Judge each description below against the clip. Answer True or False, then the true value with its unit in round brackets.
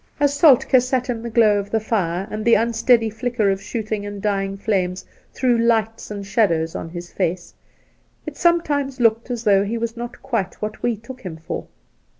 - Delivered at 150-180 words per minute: False (190 wpm)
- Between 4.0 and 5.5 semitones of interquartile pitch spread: False (3.4 semitones)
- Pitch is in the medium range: False (220 Hz)